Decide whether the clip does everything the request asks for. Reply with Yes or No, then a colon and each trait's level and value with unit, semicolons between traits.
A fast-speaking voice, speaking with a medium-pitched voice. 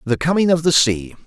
Yes: fast, 235 wpm; medium, 145 Hz